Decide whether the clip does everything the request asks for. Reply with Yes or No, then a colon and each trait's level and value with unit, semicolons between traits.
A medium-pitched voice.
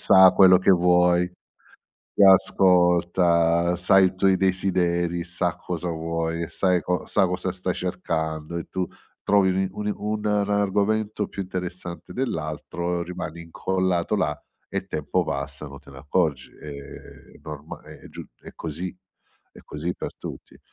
No: very low, 90 Hz